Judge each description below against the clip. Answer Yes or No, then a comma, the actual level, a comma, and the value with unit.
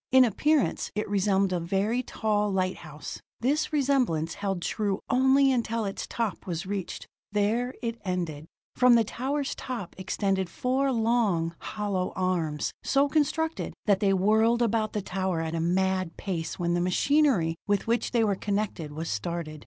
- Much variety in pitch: No, average, 4.8 semitones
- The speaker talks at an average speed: Yes, average, 160 wpm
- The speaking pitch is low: No, high, 205 Hz